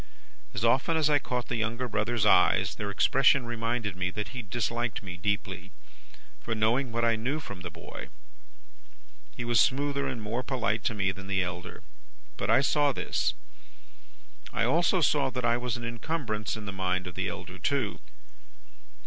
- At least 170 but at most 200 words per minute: Yes, average, 175 wpm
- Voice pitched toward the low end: Yes, low, 115 Hz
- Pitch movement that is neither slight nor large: Yes, average, 3.9 semitones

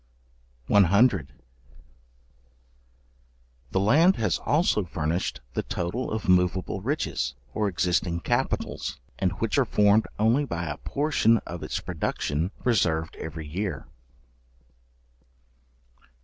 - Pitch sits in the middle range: No, very low, 95 Hz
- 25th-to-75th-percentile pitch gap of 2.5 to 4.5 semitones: No, average, 5.0 semitones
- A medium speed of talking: No, slow, 105 wpm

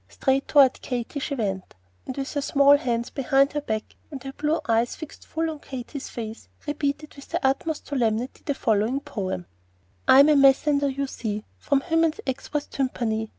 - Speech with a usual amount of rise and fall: Yes, average, 3.3 semitones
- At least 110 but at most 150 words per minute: No, average, 175 wpm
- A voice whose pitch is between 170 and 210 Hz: No, very high, 275 Hz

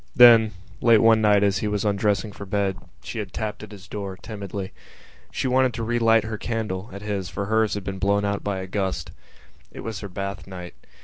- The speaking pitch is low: Yes, low, 105 Hz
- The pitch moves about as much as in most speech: No, narrow, 2.1 semitones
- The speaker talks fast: Yes, fast, 210 wpm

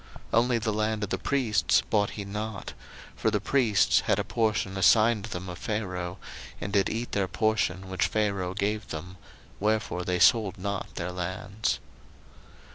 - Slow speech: No, average, 165 wpm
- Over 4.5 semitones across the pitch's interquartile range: No, average, 2.8 semitones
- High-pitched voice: No, low, 100 Hz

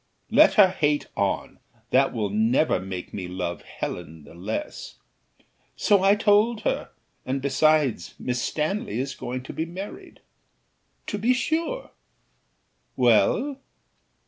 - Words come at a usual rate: No, slow, 125 wpm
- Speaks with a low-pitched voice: No, medium, 150 Hz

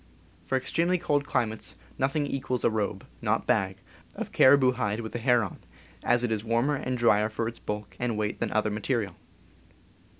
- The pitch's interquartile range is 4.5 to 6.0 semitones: No, average, 3.4 semitones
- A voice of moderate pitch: No, low, 115 Hz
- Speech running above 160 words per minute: Yes, average, 190 wpm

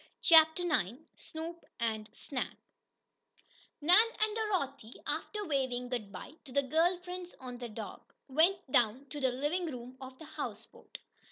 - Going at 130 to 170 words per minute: Yes, average, 150 wpm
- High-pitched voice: Yes, very high, 280 Hz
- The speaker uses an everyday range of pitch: No, wide, 5.7 semitones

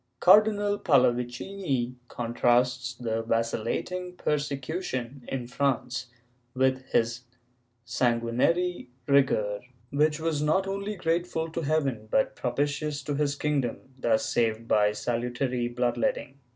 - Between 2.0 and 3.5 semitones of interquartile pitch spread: No, average, 4.7 semitones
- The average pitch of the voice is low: Yes, low, 130 Hz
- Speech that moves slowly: Yes, slow, 110 wpm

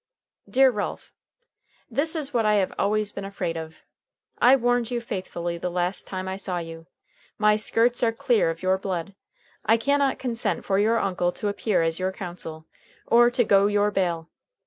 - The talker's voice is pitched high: Yes, high, 200 Hz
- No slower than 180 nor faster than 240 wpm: Yes, average, 185 wpm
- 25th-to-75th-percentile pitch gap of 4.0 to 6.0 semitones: Yes, average, 4.4 semitones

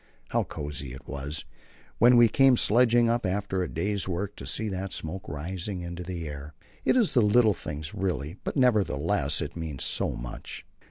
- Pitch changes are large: Yes, wide, 6.1 semitones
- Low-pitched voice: Yes, very low, 95 Hz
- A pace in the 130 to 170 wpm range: No, average, 180 wpm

